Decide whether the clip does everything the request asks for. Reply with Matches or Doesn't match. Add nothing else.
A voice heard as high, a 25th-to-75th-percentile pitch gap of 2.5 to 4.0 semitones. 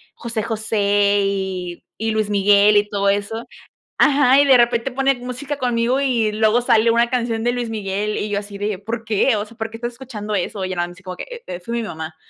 Matches